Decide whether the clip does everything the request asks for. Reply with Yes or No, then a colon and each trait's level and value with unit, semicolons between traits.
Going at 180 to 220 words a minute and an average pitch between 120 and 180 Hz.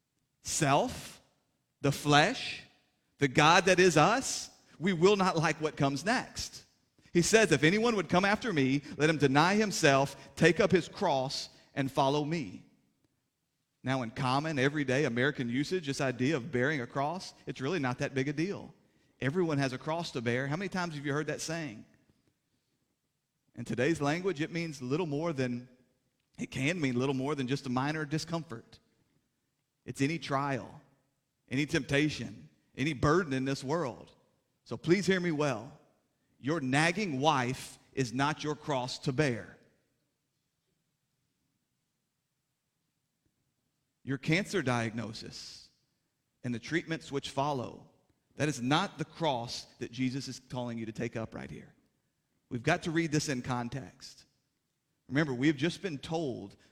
No: average, 155 wpm; medium, 140 Hz